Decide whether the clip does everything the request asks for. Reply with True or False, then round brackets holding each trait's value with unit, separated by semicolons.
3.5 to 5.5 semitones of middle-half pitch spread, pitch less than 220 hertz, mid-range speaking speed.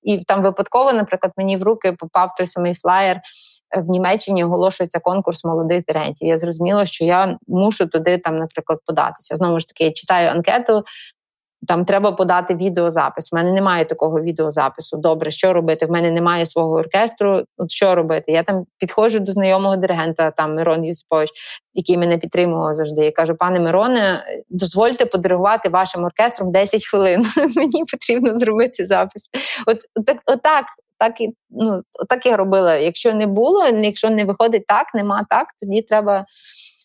False (4.0 semitones; 185 Hz; 160 wpm)